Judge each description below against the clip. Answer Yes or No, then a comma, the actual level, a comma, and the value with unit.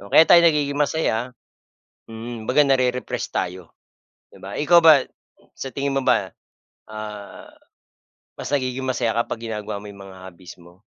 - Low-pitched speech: Yes, low, 125 Hz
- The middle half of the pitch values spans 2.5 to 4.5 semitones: No, average, 4.9 semitones